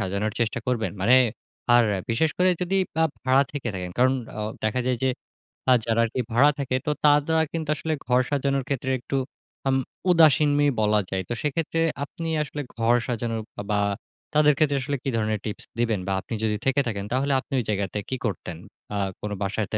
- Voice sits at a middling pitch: No, low, 125 Hz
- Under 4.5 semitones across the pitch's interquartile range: No, average, 4.9 semitones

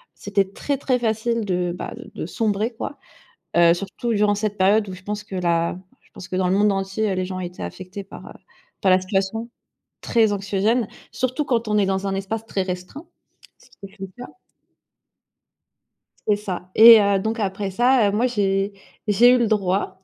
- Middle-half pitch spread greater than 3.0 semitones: No, average, 2.7 semitones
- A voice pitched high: Yes, high, 200 Hz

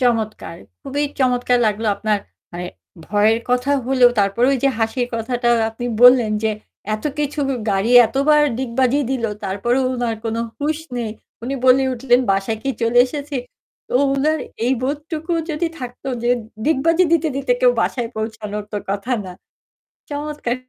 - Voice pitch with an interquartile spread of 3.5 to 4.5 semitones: Yes, average, 3.8 semitones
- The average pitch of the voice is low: No, high, 245 Hz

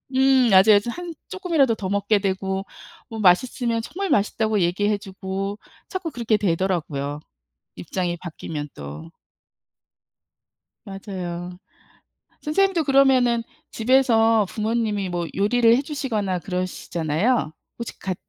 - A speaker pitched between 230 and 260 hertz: No, high, 210 Hz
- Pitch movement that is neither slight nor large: Yes, average, 4.9 semitones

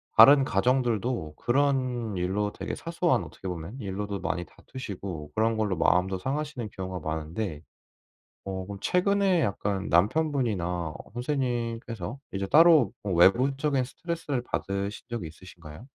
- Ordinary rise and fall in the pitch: No, wide, 6.1 semitones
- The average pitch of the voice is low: Yes, low, 110 Hz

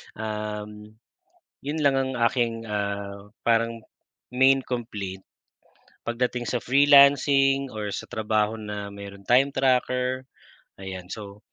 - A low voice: Yes, low, 115 Hz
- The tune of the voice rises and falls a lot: No, average, 4.1 semitones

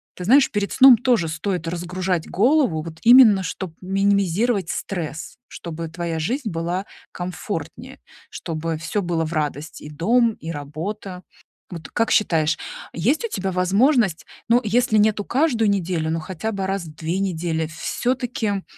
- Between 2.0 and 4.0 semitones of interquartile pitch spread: No, average, 4.9 semitones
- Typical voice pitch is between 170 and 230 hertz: Yes, medium, 185 Hz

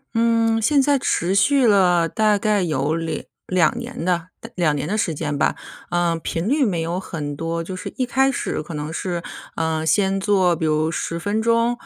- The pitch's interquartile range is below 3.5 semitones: No, average, 5.1 semitones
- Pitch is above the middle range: No, medium, 180 Hz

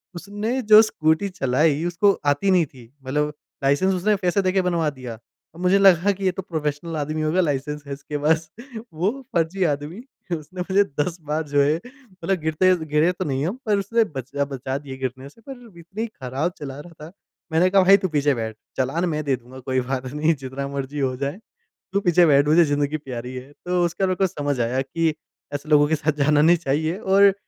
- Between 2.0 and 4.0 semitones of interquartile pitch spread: No, average, 4.8 semitones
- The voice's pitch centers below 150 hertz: No, medium, 155 Hz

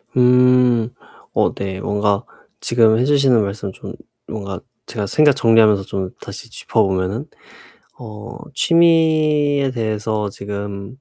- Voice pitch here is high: No, low, 110 Hz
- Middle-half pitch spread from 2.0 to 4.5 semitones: Yes, average, 4.2 semitones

